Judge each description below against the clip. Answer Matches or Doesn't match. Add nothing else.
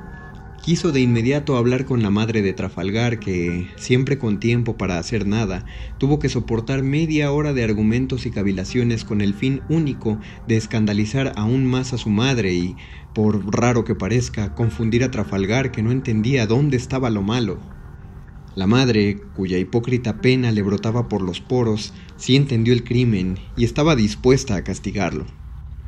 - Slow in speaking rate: Doesn't match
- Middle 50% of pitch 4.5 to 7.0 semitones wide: Doesn't match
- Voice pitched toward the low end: Matches